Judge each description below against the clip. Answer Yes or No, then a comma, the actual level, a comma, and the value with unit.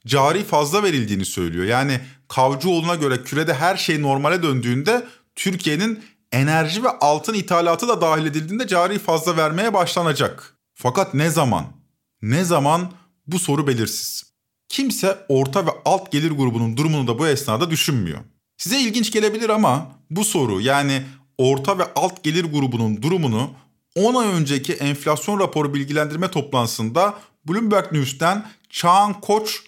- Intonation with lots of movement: Yes, wide, 5.9 semitones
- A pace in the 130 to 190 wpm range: Yes, average, 135 wpm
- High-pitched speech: No, medium, 155 Hz